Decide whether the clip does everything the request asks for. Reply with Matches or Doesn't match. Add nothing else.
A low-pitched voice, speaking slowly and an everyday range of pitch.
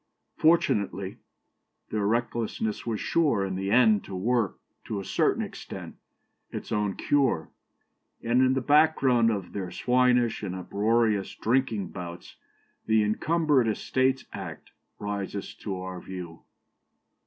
Matches